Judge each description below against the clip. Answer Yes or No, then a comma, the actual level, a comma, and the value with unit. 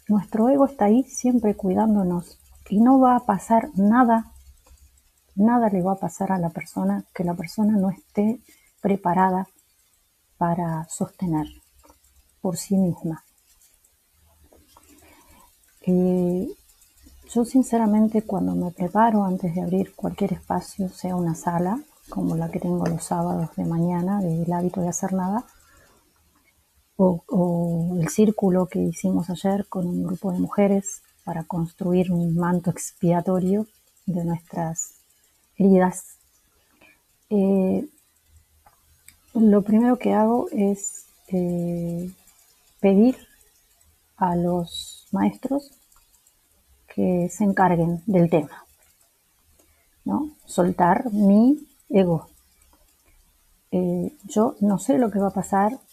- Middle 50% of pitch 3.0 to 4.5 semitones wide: Yes, average, 3.6 semitones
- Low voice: No, medium, 185 Hz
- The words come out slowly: Yes, slow, 115 wpm